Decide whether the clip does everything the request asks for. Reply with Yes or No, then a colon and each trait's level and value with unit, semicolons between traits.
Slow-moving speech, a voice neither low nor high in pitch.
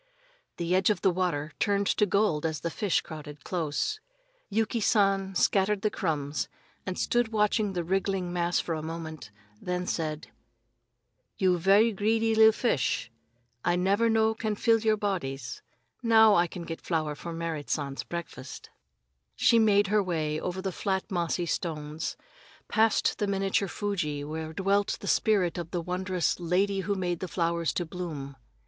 No: average, 160 wpm; medium, 180 Hz